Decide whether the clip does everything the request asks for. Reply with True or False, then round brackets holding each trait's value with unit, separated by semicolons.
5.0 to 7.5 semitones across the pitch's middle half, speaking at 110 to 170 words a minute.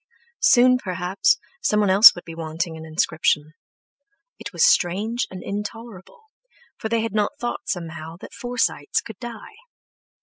True (5.5 semitones; 140 wpm)